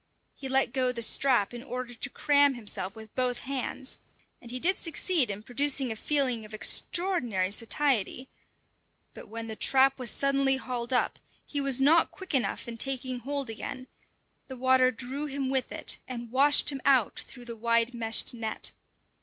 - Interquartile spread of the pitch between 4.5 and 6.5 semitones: No, average, 2.7 semitones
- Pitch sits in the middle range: No, very high, 255 Hz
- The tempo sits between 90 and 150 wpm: No, average, 175 wpm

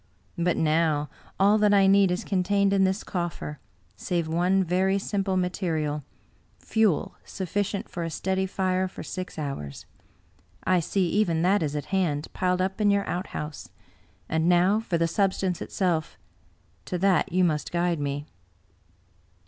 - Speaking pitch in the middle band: Yes, medium, 180 Hz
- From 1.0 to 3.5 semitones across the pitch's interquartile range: Yes, average, 2.8 semitones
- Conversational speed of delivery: Yes, average, 155 wpm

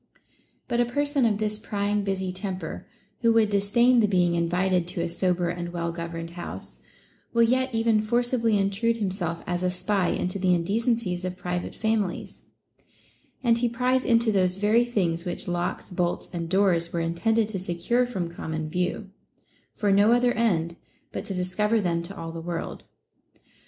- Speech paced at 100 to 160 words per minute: No, average, 170 wpm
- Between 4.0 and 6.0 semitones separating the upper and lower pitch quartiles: Yes, average, 4.5 semitones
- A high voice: Yes, high, 195 Hz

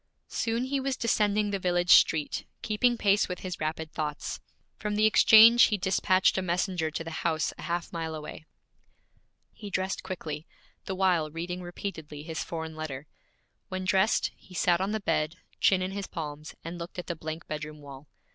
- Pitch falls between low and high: Yes, medium, 175 Hz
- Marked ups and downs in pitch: No, average, 3.8 semitones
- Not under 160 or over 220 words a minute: Yes, average, 180 wpm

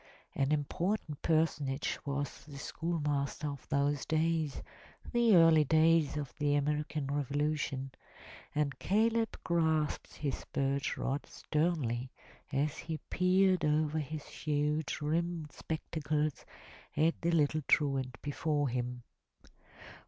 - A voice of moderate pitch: Yes, medium, 150 Hz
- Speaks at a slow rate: Yes, slow, 115 wpm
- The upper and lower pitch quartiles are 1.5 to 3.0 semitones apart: Yes, narrow, 2.4 semitones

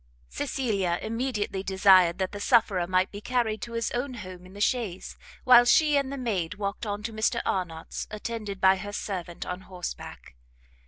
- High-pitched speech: Yes, high, 205 Hz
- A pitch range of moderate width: Yes, average, 3.9 semitones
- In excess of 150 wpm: Yes, average, 175 wpm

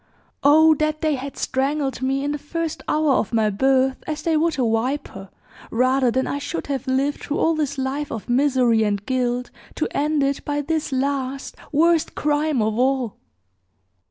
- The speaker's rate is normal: Yes, average, 180 wpm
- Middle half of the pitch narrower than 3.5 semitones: Yes, narrow, 2.6 semitones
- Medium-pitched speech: No, very high, 275 Hz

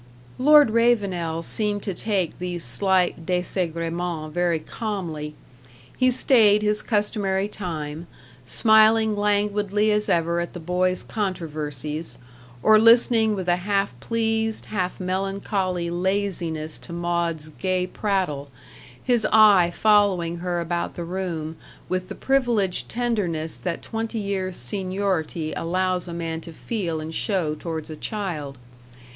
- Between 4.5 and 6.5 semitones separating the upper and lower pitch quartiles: No, average, 3.8 semitones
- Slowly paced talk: Yes, slow, 125 wpm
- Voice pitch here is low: No, medium, 185 Hz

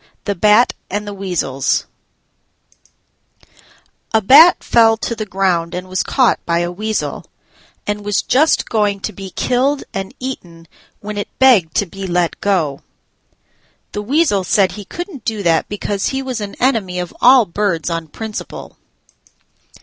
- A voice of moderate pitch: No, high, 205 Hz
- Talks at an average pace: Yes, average, 150 wpm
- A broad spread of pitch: No, average, 4.1 semitones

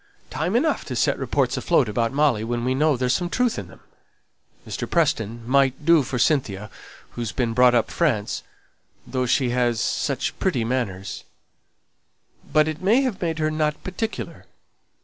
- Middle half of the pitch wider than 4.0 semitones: Yes, average, 5.1 semitones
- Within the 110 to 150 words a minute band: No, average, 170 wpm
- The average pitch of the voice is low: Yes, low, 130 Hz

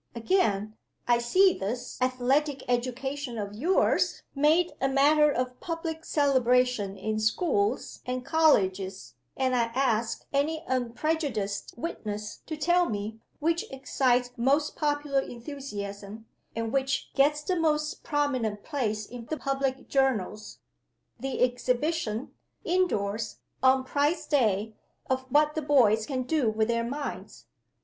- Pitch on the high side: Yes, very high, 260 Hz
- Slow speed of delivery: Yes, slow, 125 wpm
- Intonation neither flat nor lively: Yes, average, 4.8 semitones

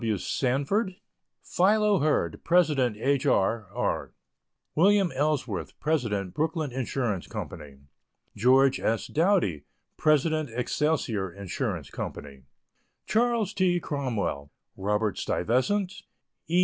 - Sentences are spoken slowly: Yes, slow, 95 wpm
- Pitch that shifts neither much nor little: No, wide, 7.7 semitones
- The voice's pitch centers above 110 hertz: Yes, medium, 140 Hz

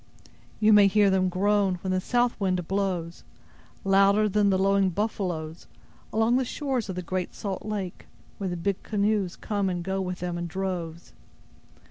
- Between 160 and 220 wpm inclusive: Yes, average, 170 wpm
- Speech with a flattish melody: Yes, narrow, 2.2 semitones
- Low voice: No, high, 195 Hz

